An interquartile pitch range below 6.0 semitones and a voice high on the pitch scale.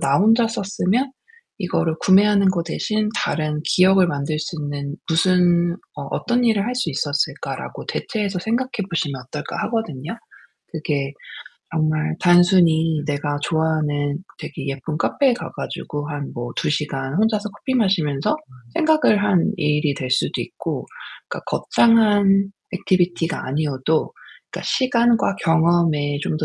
No: wide, 5.5 semitones; medium, 170 Hz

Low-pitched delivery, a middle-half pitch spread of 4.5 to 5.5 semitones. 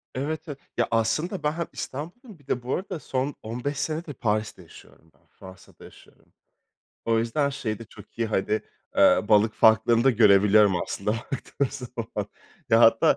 Yes: low, 115 Hz; average, 5.0 semitones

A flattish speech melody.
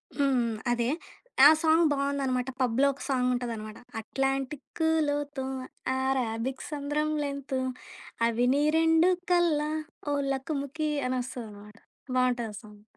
No: average, 3.0 semitones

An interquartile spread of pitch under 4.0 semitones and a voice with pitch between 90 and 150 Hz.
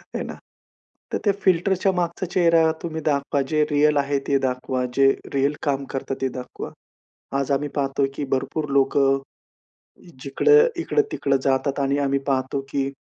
Yes: average, 2.8 semitones; medium, 140 Hz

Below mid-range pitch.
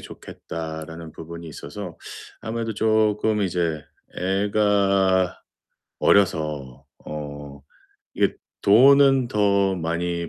Yes: very low, 95 Hz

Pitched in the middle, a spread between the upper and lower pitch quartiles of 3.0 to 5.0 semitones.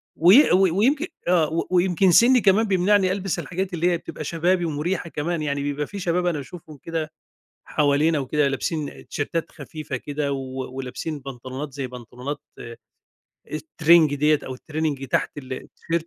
Yes: medium, 155 Hz; average, 3.9 semitones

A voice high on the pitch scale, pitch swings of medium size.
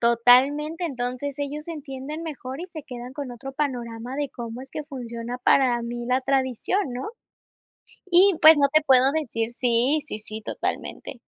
Yes: very high, 265 Hz; average, 3.6 semitones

